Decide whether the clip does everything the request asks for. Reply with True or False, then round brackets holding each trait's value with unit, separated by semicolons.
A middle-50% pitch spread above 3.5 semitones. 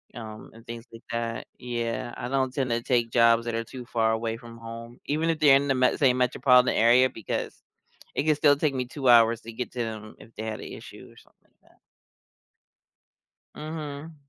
False (2.7 semitones)